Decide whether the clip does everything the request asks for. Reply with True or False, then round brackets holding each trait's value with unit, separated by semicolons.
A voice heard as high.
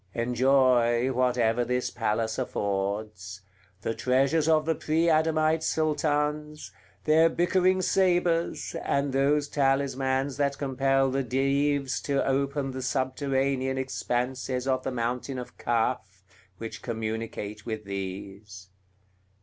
False (130 Hz)